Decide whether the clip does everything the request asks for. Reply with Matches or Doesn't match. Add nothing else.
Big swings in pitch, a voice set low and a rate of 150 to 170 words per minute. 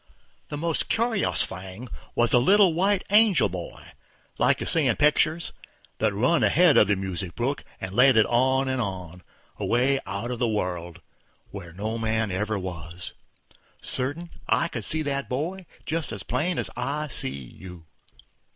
Matches